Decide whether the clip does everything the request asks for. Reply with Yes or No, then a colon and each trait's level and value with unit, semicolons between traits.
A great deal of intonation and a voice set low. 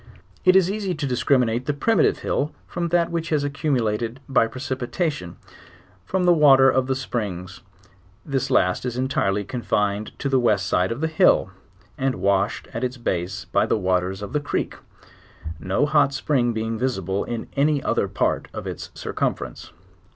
Yes: wide, 5.7 semitones; low, 130 Hz